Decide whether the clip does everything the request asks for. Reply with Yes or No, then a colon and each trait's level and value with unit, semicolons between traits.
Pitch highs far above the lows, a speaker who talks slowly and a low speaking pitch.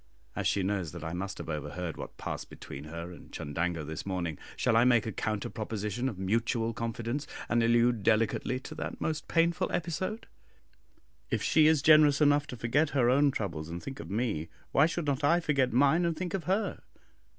No: wide, 7.4 semitones; average, 195 wpm; low, 115 Hz